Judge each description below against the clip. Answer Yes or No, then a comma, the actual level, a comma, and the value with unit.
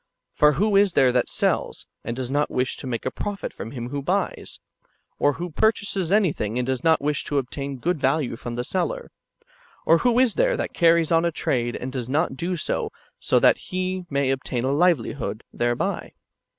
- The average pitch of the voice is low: No, medium, 145 Hz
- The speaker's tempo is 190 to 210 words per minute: Yes, average, 200 wpm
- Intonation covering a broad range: Yes, wide, 6.0 semitones